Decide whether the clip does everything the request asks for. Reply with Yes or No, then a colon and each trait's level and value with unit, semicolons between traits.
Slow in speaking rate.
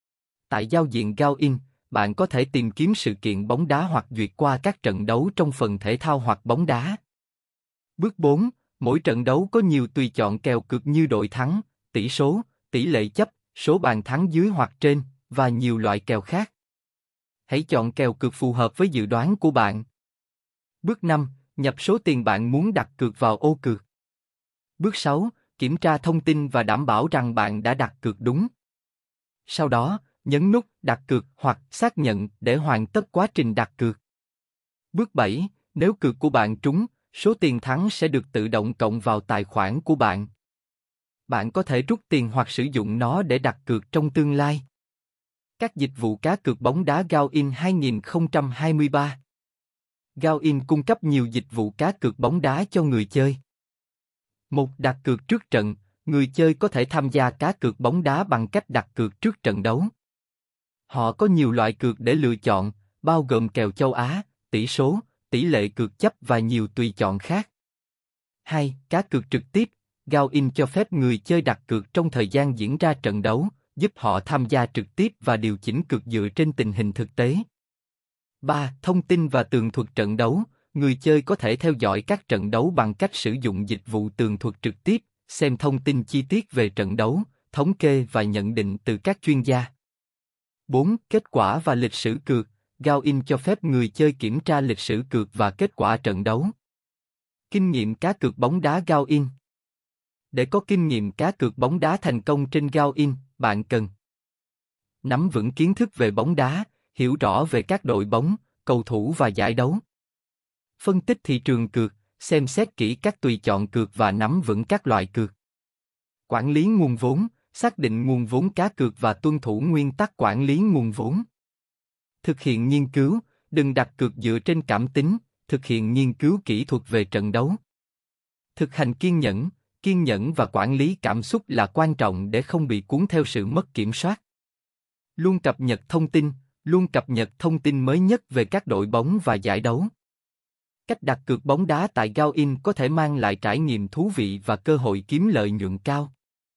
No: average, 195 wpm